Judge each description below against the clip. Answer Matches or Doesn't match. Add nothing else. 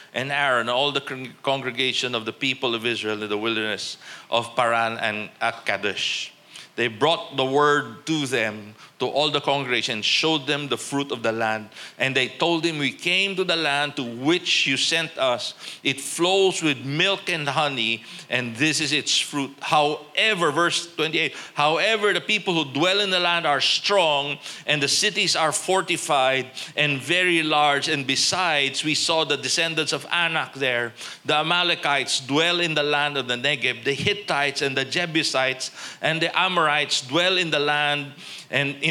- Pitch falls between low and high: Matches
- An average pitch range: Matches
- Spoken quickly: Matches